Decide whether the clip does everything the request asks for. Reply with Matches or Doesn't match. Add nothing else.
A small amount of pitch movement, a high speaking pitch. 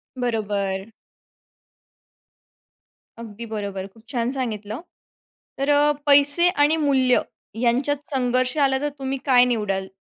Doesn't match